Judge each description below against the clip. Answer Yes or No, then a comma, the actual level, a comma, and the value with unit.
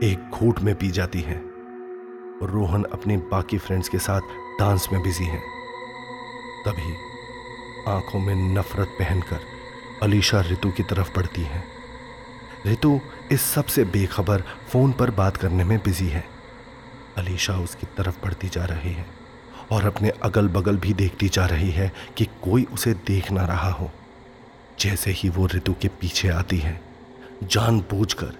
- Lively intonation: No, average, 4.1 semitones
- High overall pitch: No, low, 100 Hz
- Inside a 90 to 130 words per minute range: No, average, 150 wpm